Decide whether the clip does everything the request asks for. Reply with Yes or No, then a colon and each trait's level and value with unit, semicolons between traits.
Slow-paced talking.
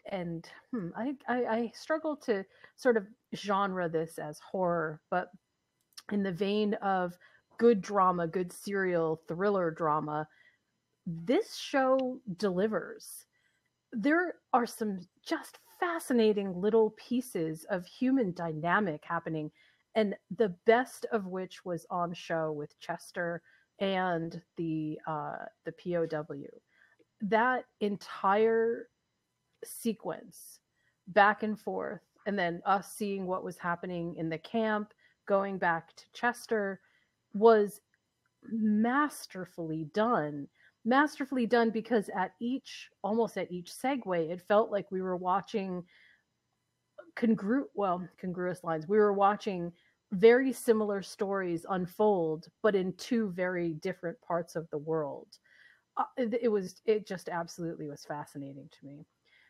Yes: slow, 120 wpm